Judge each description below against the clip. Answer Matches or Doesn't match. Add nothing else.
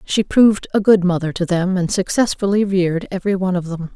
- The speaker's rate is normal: Doesn't match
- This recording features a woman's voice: Matches